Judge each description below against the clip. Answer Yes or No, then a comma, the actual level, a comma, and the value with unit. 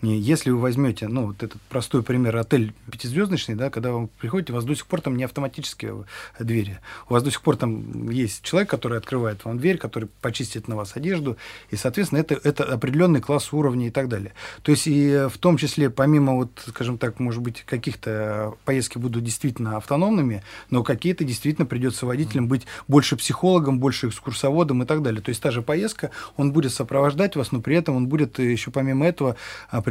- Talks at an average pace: No, fast, 195 wpm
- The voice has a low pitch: Yes, low, 130 Hz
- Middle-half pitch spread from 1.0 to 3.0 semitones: No, average, 3.7 semitones